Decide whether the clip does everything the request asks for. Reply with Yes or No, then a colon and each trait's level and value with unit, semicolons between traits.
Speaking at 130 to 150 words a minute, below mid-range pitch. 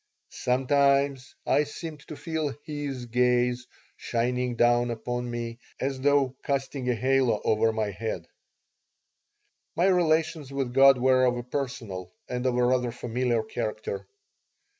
Yes: slow, 135 wpm; low, 125 Hz